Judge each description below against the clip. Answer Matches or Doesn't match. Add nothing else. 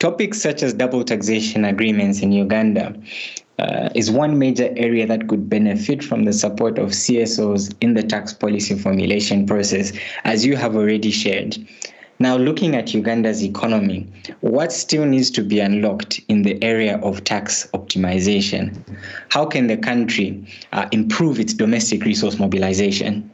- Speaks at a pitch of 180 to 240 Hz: Doesn't match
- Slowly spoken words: Doesn't match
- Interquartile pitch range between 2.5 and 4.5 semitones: Doesn't match